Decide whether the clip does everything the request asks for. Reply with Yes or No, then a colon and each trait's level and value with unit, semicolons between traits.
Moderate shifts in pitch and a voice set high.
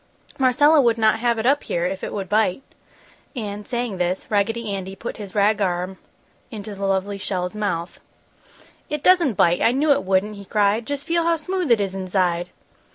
Yes: average, 4.3 semitones; high, 210 Hz